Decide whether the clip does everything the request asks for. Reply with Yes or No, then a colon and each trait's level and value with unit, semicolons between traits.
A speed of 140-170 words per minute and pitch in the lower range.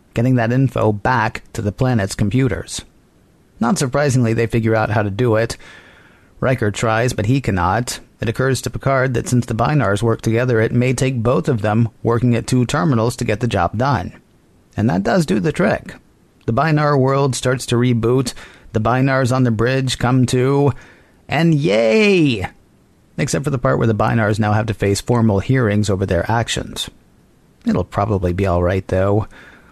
No: average, 180 wpm; low, 120 Hz